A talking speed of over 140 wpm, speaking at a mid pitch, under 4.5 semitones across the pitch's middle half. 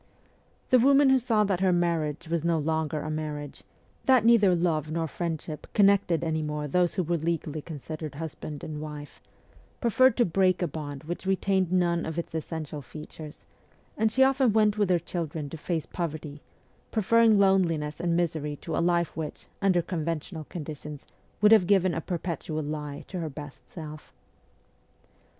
Yes: average, 170 wpm; medium, 165 Hz; average, 3.7 semitones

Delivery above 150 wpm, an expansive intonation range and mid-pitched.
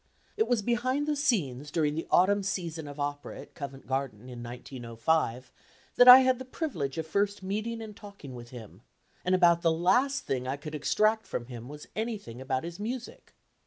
Yes: average, 190 wpm; wide, 8.5 semitones; medium, 165 Hz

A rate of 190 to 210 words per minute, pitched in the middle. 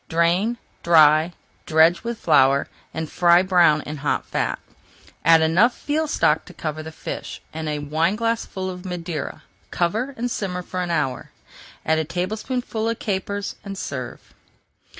No: average, 150 wpm; medium, 175 Hz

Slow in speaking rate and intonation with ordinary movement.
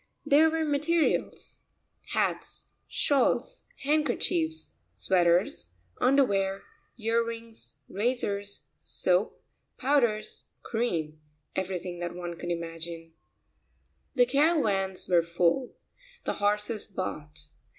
No: slow, 90 wpm; wide, 7.0 semitones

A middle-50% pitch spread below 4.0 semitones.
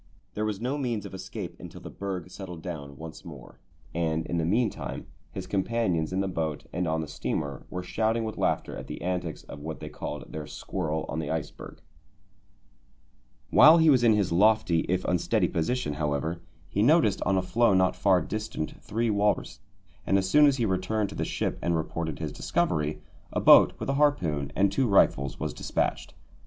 No: average, 5.1 semitones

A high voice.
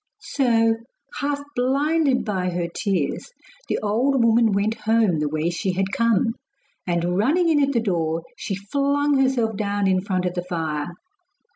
Yes: high, 210 Hz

